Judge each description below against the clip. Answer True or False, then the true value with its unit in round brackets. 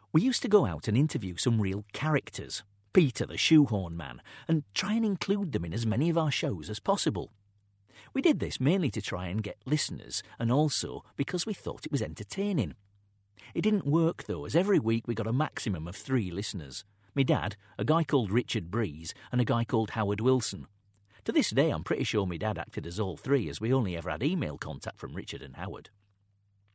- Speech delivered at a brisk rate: True (210 wpm)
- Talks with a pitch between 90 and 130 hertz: True (110 Hz)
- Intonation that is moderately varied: False (6.6 semitones)